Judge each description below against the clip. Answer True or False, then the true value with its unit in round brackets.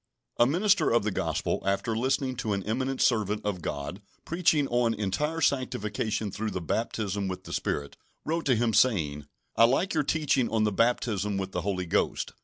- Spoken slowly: False (185 wpm)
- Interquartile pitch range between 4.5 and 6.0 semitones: True (4.8 semitones)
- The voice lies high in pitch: False (110 Hz)